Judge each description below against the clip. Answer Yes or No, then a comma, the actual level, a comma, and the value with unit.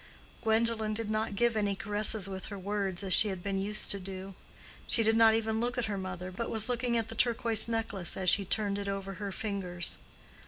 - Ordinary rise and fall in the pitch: No, narrow, 2.3 semitones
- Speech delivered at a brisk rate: Yes, fast, 220 wpm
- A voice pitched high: Yes, high, 210 Hz